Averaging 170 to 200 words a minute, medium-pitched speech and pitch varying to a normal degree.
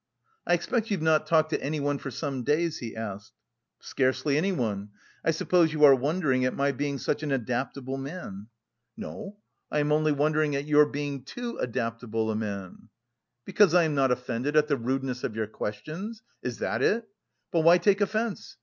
Yes: average, 180 wpm; medium, 145 Hz; average, 4.3 semitones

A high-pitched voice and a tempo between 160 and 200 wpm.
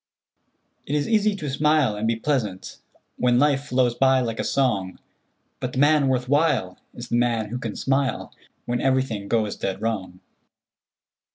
No: low, 125 Hz; average, 165 wpm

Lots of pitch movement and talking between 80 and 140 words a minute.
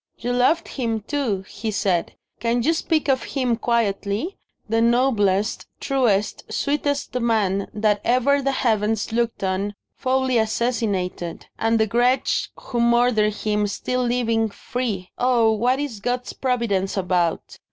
No: average, 3.4 semitones; slow, 135 wpm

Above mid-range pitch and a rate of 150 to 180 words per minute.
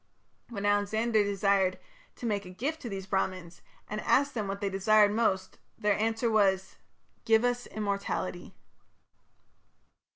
No: high, 205 Hz; average, 140 wpm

